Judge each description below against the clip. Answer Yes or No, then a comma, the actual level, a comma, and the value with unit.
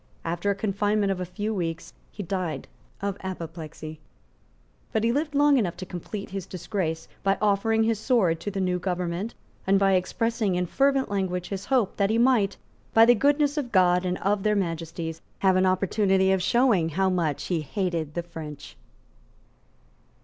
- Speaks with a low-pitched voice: No, high, 190 Hz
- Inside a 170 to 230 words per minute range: Yes, average, 175 wpm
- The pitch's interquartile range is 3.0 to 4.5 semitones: Yes, average, 3.3 semitones